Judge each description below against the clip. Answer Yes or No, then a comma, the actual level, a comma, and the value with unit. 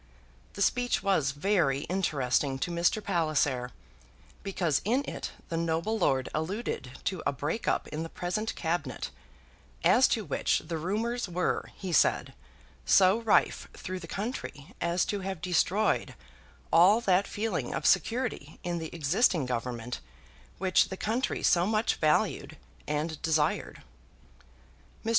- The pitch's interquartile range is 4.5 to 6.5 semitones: Yes, average, 5.0 semitones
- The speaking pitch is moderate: Yes, medium, 175 Hz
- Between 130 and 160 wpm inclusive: Yes, average, 140 wpm